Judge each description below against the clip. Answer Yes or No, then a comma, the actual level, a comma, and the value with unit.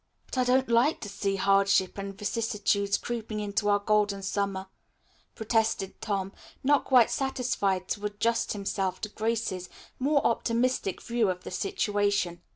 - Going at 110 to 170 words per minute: Yes, average, 145 wpm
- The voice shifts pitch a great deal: No, average, 2.9 semitones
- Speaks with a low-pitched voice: No, high, 205 Hz